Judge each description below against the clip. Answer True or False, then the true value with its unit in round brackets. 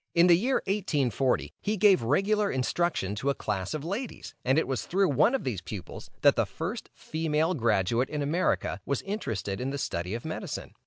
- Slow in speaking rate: False (195 wpm)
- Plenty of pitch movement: True (8.0 semitones)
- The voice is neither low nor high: True (145 Hz)